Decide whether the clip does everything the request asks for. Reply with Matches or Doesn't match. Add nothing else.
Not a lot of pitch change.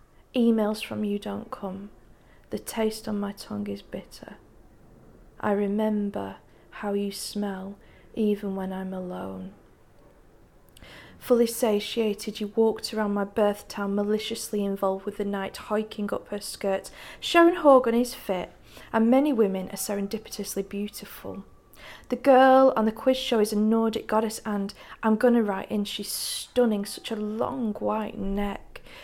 Matches